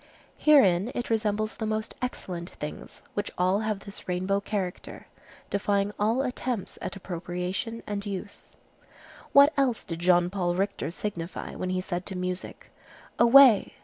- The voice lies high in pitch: Yes, high, 200 Hz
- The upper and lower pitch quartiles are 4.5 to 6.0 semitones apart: No, average, 3.2 semitones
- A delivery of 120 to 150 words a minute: Yes, average, 145 wpm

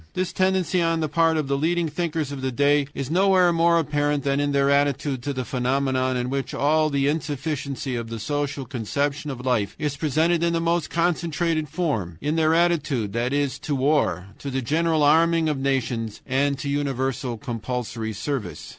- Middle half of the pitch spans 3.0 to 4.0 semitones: Yes, average, 3.5 semitones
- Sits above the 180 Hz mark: No, medium, 145 Hz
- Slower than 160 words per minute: No, average, 190 wpm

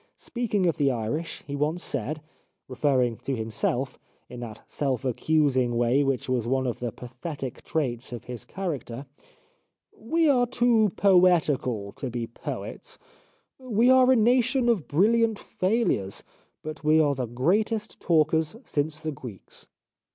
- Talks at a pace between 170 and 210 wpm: No, average, 150 wpm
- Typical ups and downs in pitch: No, wide, 8.4 semitones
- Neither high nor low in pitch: Yes, medium, 150 Hz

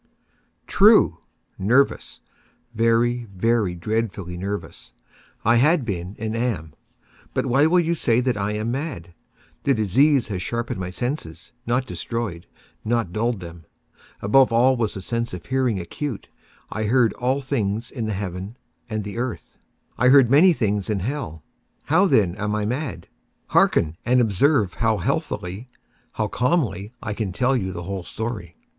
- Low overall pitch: Yes, low, 115 Hz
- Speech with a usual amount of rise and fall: Yes, average, 4.5 semitones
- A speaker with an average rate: Yes, average, 145 wpm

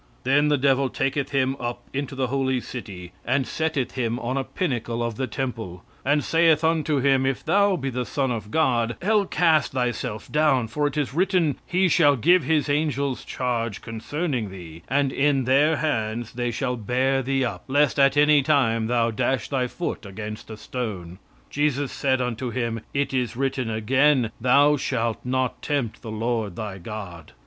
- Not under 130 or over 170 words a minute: No, average, 180 wpm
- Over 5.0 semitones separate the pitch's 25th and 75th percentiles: No, average, 3.8 semitones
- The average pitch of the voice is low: Yes, low, 130 Hz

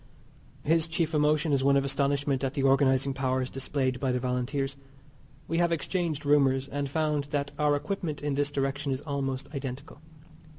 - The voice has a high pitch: No, medium, 140 Hz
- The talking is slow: No, average, 170 wpm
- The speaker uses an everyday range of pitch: No, narrow, 1.8 semitones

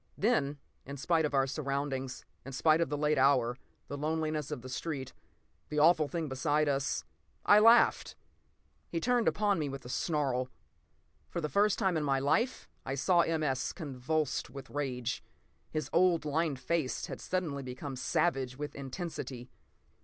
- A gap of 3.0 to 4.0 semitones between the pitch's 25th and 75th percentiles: Yes, average, 3.5 semitones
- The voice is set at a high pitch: No, medium, 145 Hz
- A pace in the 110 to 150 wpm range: No, average, 165 wpm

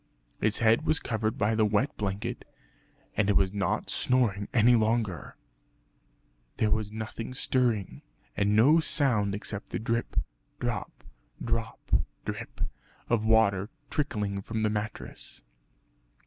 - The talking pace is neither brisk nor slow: No, slow, 125 wpm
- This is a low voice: Yes, low, 110 Hz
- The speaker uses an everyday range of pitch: No, narrow, 2.2 semitones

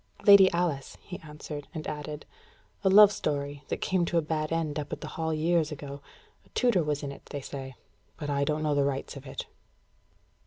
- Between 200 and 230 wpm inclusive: Yes, fast, 205 wpm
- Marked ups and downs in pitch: No, average, 2.8 semitones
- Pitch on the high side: No, medium, 150 Hz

